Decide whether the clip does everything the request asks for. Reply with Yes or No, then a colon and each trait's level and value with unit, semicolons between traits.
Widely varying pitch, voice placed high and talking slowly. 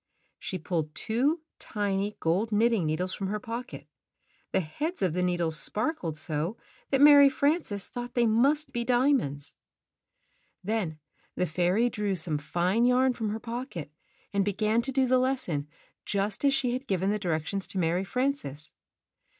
No: wide, 6.0 semitones; high, 210 Hz; average, 160 wpm